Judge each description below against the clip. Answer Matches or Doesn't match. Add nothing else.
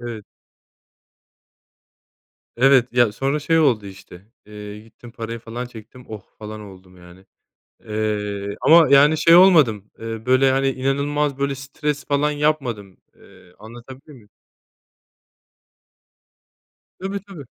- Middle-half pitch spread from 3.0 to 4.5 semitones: Doesn't match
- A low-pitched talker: Matches